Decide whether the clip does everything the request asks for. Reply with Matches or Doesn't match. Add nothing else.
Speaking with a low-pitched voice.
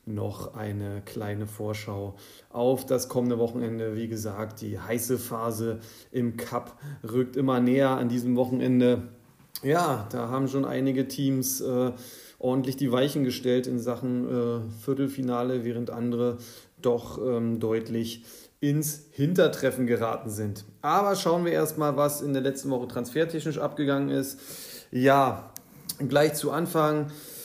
Matches